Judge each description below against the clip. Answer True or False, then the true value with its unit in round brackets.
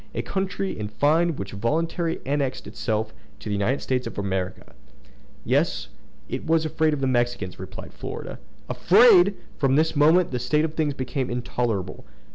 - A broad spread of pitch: True (6.1 semitones)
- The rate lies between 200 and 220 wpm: False (165 wpm)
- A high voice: False (135 Hz)